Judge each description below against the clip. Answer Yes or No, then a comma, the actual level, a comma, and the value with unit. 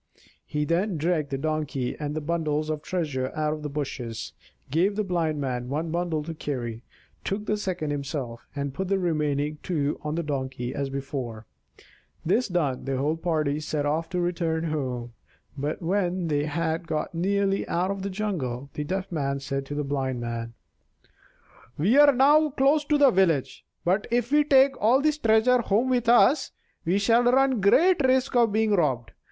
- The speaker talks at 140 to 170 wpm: No, average, 180 wpm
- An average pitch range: No, wide, 6.0 semitones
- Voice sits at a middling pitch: Yes, medium, 160 Hz